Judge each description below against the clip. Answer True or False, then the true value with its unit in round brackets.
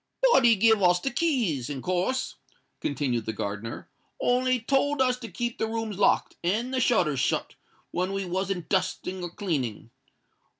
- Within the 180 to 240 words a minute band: False (170 wpm)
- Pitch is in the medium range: False (195 Hz)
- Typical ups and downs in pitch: False (6.3 semitones)